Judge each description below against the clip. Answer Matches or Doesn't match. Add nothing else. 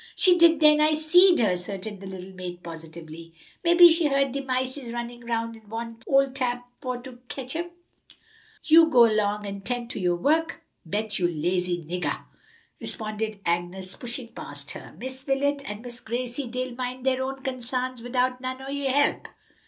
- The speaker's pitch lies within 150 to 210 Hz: Doesn't match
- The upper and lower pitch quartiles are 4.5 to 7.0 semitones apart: Matches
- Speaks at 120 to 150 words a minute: Doesn't match